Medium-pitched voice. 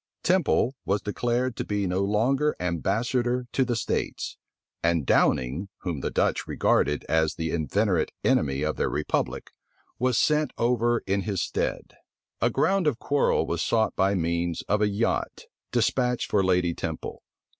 No: low, 105 Hz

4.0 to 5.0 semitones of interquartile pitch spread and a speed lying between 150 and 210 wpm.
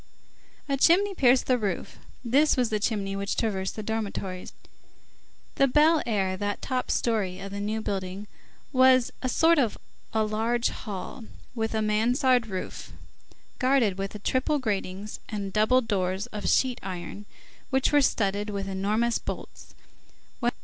No: average, 4.3 semitones; average, 140 wpm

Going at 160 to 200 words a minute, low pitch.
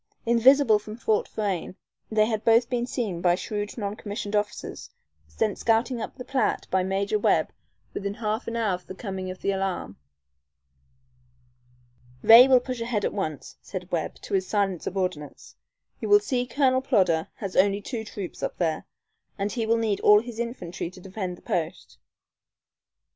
No: average, 170 wpm; high, 210 Hz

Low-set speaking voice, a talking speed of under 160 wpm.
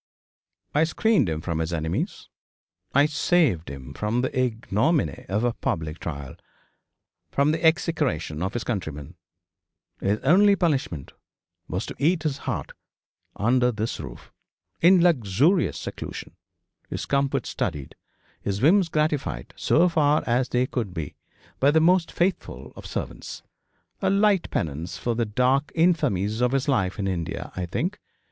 Yes: low, 125 Hz; average, 145 wpm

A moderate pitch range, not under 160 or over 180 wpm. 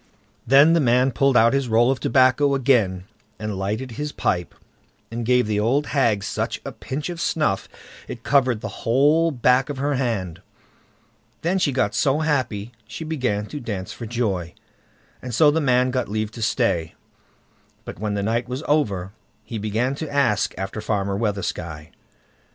Yes: average, 4.8 semitones; average, 170 wpm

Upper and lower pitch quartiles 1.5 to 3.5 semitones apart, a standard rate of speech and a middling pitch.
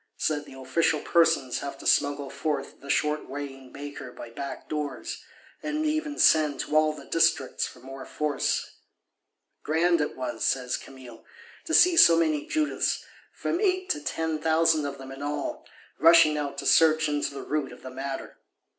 Yes: average, 2.9 semitones; average, 175 wpm; medium, 150 Hz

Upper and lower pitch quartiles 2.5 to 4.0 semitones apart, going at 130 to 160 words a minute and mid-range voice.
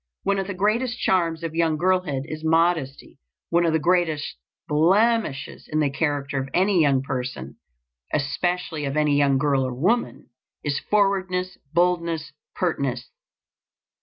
No: average, 4.4 semitones; average, 140 wpm; medium, 160 Hz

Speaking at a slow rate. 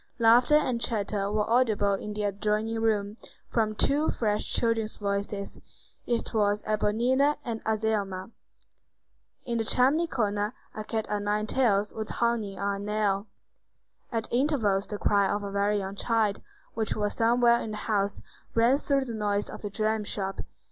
No: average, 160 wpm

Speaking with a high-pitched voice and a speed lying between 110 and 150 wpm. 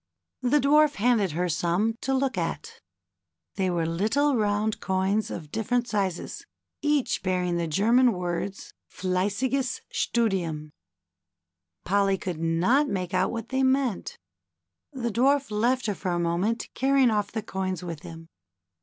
Yes: high, 205 Hz; average, 145 wpm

